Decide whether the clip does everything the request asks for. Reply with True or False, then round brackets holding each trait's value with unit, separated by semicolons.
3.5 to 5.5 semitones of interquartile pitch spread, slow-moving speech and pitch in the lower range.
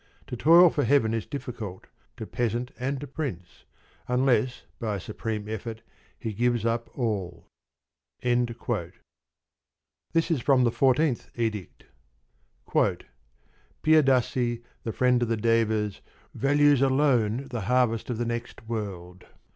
False (3.0 semitones; 125 wpm; 120 Hz)